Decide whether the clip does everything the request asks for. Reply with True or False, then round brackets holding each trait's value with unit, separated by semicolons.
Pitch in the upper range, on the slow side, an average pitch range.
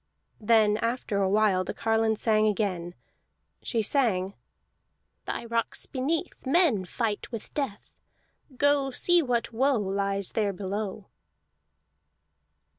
True (220 Hz; 115 wpm; 3.8 semitones)